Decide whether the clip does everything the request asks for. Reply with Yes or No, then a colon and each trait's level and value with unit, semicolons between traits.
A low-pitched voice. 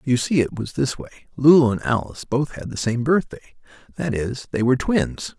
Yes: low, 130 Hz